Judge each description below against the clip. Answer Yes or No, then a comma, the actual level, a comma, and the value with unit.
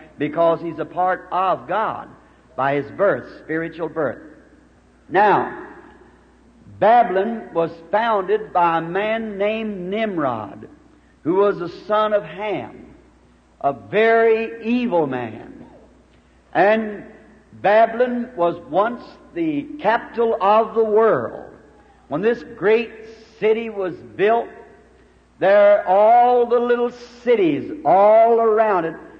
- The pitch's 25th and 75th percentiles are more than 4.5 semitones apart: Yes, average, 4.9 semitones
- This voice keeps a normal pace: No, slow, 110 wpm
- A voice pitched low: No, high, 215 Hz